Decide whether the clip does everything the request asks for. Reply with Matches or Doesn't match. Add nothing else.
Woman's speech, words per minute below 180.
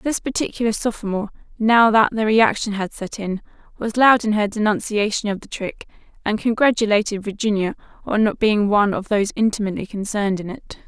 Matches